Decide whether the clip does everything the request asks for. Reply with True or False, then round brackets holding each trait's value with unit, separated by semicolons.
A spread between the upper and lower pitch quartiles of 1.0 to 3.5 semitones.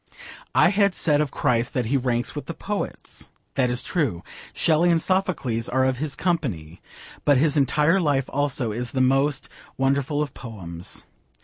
False (3.9 semitones)